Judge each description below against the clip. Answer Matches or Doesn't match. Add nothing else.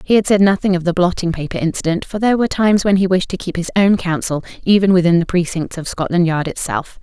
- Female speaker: Matches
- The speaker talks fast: Matches